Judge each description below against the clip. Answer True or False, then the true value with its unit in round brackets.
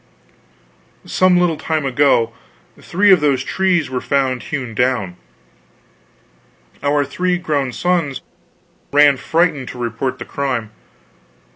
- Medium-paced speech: False (115 wpm)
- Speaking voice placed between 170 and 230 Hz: False (140 Hz)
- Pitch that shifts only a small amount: False (4.5 semitones)